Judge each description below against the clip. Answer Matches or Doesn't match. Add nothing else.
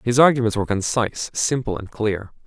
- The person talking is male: Matches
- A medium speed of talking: Matches